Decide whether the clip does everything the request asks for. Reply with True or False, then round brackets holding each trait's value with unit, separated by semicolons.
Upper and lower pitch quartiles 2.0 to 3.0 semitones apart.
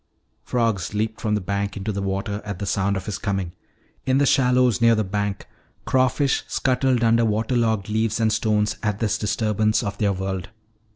True (2.4 semitones)